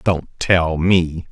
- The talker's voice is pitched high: No, very low, 85 Hz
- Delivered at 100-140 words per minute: Yes, slow, 135 wpm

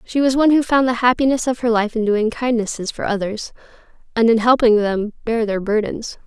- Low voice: No, high, 230 Hz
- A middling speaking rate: No, fast, 210 wpm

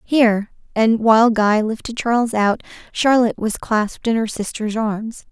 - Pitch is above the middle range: Yes, high, 225 Hz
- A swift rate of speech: No, average, 160 wpm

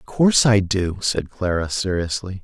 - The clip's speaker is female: No, male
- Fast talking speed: No, average, 175 wpm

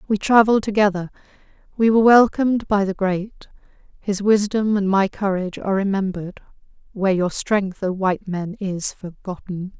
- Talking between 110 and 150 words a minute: Yes, average, 145 wpm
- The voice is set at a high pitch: Yes, high, 200 Hz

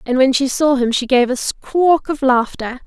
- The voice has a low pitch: No, very high, 265 Hz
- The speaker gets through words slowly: No, fast, 230 wpm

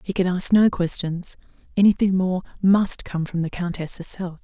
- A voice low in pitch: No, medium, 180 Hz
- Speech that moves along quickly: No, average, 160 wpm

